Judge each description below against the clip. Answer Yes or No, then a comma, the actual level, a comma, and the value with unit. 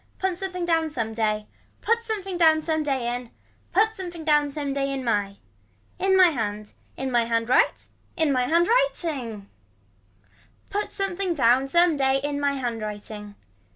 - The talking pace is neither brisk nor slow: Yes, average, 165 wpm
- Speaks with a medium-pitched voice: No, very high, 285 Hz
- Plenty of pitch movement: Yes, wide, 6.8 semitones